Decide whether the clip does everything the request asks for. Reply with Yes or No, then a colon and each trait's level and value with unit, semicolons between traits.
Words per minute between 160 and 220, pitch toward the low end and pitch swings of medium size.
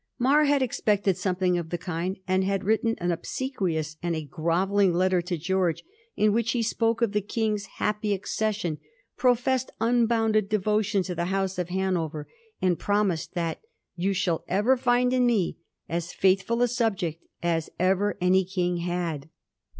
No: average, 170 wpm; high, 190 Hz; average, 3.9 semitones